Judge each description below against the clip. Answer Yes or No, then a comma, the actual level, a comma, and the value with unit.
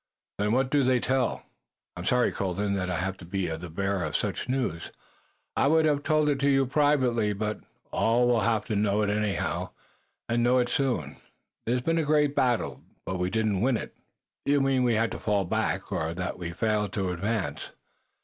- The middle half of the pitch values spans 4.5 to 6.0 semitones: Yes, average, 5.2 semitones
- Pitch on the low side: Yes, low, 110 Hz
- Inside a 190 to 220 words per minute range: Yes, fast, 205 wpm